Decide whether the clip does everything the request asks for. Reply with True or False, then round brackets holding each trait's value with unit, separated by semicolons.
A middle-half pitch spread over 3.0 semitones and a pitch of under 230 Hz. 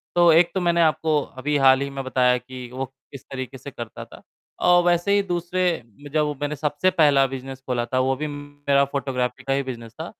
True (3.6 semitones; 140 Hz)